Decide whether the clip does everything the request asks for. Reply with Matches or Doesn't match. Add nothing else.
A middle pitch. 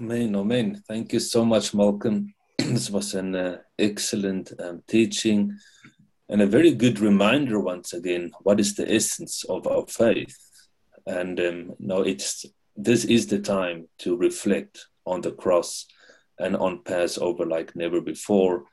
Doesn't match